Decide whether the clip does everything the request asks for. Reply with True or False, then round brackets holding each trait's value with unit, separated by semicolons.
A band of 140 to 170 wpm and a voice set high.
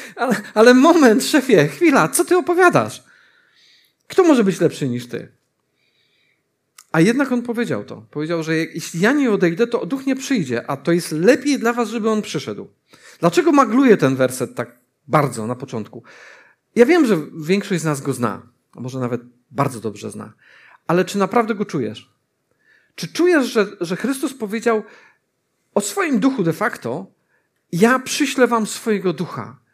True (160 wpm; 205 Hz)